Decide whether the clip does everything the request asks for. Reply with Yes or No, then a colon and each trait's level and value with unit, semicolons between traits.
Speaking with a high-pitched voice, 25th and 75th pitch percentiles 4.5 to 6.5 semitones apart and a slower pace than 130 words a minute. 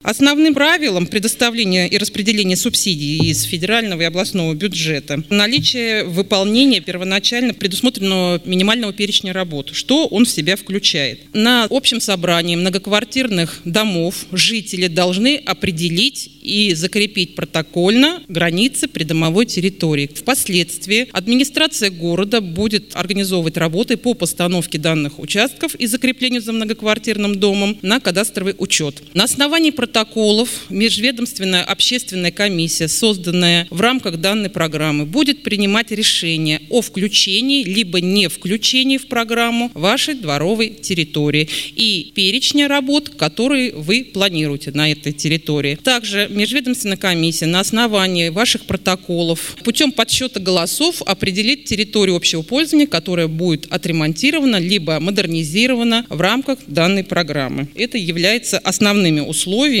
Yes: high, 195 Hz; average, 5.2 semitones; average, 115 wpm